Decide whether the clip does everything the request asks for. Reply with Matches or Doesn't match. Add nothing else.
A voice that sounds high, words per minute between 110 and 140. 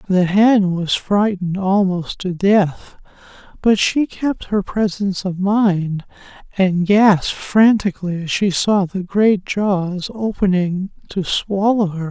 Matches